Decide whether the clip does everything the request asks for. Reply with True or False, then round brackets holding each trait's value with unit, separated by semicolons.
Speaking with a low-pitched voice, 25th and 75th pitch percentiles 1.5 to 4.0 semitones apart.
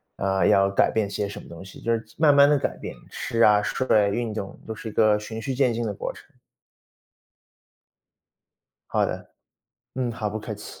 True (110 Hz; 2.6 semitones)